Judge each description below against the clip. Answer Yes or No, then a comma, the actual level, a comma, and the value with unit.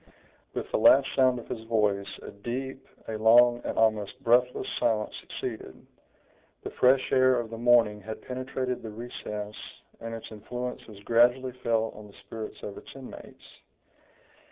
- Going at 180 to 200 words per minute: No, average, 155 wpm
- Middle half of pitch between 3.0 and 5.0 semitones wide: No, narrow, 2.6 semitones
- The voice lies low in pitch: Yes, low, 115 Hz